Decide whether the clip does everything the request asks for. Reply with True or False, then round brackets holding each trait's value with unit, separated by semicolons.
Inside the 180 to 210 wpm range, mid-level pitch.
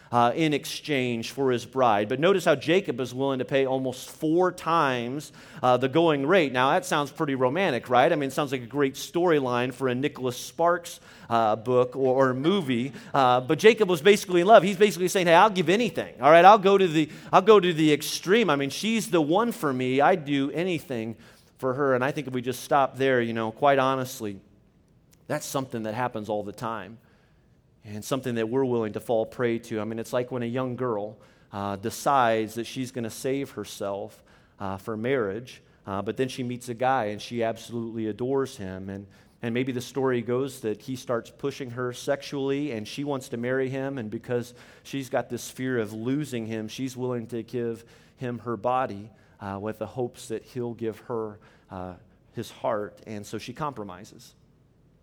False (205 wpm; 125 Hz)